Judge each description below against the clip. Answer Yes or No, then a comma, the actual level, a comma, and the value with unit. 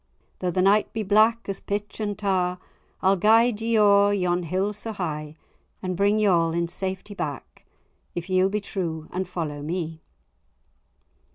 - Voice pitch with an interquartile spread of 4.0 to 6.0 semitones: No, average, 3.0 semitones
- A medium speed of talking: Yes, average, 165 wpm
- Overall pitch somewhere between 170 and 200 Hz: Yes, high, 190 Hz